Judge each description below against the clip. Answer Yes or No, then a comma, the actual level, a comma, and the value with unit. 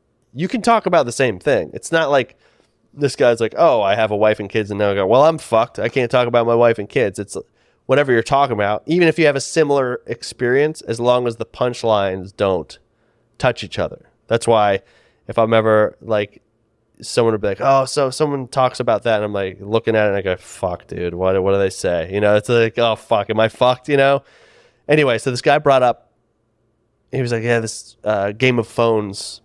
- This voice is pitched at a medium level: No, low, 115 Hz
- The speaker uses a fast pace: Yes, fast, 230 wpm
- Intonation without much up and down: No, average, 3.3 semitones